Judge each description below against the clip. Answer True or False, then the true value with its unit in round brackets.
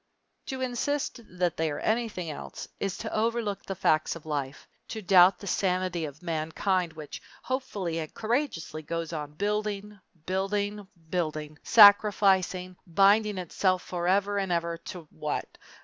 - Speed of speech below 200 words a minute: True (140 wpm)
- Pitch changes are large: False (3.8 semitones)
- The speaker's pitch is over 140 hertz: True (185 Hz)